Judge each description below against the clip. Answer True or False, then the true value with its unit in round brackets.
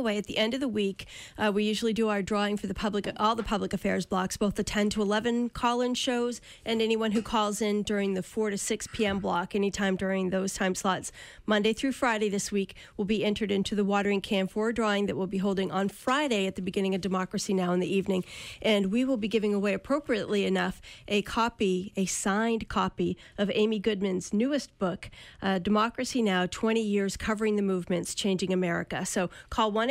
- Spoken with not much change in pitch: True (2.3 semitones)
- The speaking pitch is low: False (205 Hz)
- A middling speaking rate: False (210 wpm)